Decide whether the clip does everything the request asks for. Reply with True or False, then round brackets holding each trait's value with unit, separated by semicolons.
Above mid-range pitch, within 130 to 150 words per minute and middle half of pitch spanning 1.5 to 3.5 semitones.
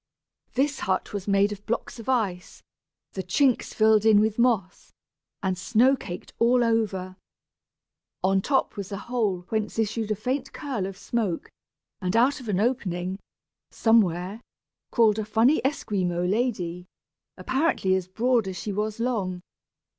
False (215 Hz; 145 wpm; 4.0 semitones)